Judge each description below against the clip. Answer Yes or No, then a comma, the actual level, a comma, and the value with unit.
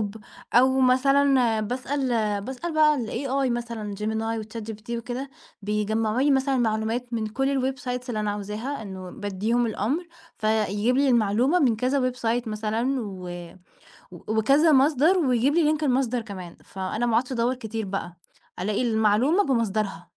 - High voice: Yes, high, 235 Hz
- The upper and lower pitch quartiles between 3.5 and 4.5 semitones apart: Yes, average, 3.8 semitones